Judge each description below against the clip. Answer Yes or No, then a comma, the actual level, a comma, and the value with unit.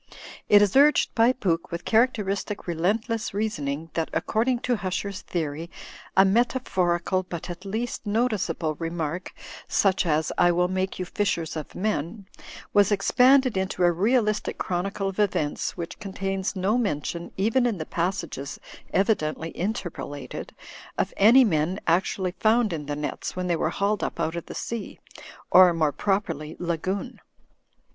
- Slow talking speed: No, average, 155 wpm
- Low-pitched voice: No, high, 190 Hz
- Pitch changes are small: No, average, 3.9 semitones